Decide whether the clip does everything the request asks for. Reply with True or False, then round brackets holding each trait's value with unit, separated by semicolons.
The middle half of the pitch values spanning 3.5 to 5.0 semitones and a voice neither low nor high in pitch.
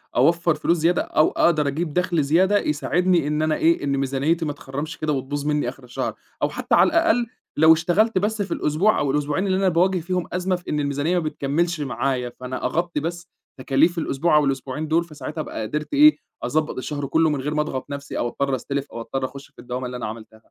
True (3.9 semitones; 150 Hz)